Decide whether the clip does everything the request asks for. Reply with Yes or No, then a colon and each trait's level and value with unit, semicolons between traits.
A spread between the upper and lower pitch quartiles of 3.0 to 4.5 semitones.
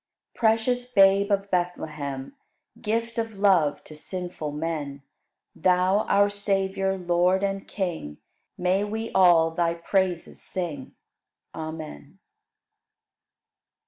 Yes: average, 3.5 semitones